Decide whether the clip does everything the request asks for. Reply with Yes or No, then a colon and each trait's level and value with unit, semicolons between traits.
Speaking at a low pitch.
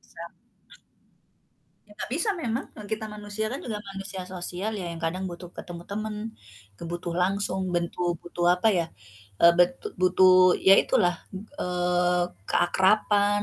No: high, 190 Hz